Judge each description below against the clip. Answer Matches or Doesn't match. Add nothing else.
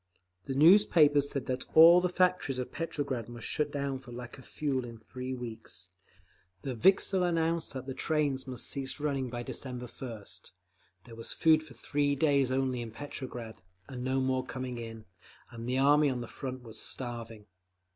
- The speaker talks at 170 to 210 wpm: Matches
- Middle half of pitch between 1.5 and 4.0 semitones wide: Matches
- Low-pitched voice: Matches